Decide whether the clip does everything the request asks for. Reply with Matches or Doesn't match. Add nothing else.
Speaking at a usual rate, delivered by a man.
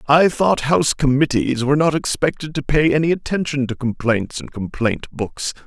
Matches